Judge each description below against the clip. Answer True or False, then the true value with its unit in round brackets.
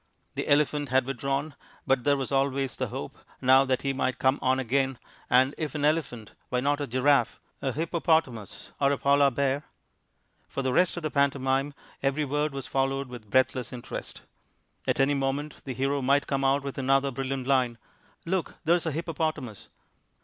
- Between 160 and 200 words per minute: True (180 wpm)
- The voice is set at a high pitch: False (135 Hz)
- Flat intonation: True (1.7 semitones)